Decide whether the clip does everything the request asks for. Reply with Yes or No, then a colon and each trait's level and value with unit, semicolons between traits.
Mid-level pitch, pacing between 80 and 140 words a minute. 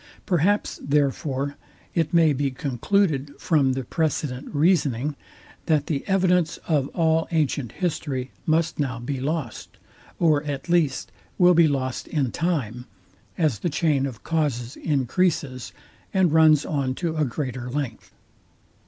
Yes: medium, 145 Hz; slow, 135 wpm